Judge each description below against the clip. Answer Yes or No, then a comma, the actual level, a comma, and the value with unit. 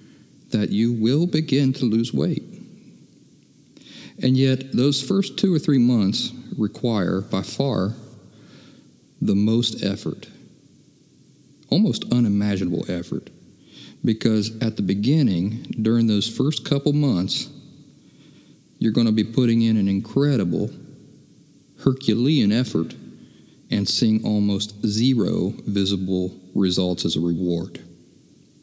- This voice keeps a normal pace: No, slow, 110 wpm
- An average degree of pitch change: Yes, average, 4.8 semitones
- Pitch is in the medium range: No, low, 110 Hz